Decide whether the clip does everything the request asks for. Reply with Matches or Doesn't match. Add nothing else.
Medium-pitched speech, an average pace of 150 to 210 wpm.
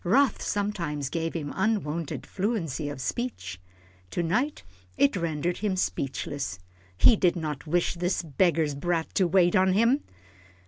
Doesn't match